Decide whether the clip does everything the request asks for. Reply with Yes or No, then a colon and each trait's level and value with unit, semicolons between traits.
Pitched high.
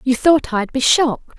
Yes: very high, 265 Hz